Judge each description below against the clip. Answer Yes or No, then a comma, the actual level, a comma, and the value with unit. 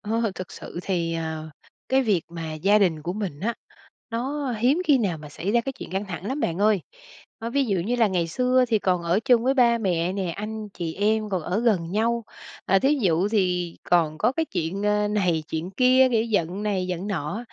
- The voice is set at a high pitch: Yes, high, 200 Hz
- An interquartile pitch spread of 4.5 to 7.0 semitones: Yes, average, 5.0 semitones